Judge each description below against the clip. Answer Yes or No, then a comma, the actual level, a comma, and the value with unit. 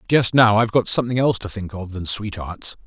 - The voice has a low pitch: Yes, low, 105 Hz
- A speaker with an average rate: No, fast, 230 wpm